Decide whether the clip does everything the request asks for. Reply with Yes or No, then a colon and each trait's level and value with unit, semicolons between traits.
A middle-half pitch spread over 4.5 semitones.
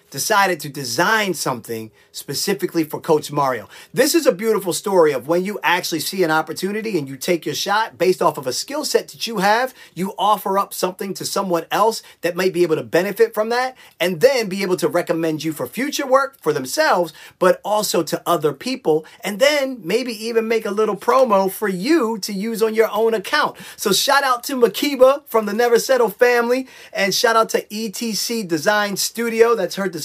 Yes: average, 5.1 semitones